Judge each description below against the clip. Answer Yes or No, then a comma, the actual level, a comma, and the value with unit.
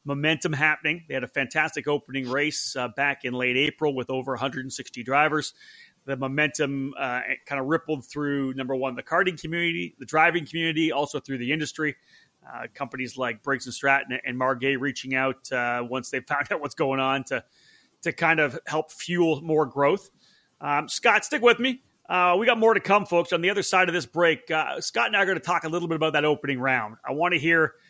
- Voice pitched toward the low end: No, medium, 150 Hz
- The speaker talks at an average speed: No, fast, 215 wpm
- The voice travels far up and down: No, average, 3.7 semitones